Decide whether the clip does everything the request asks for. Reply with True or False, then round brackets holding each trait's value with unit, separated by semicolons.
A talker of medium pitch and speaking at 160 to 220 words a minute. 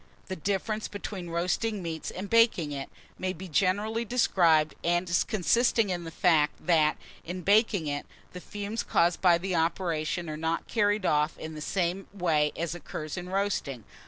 True (175 Hz; 165 wpm)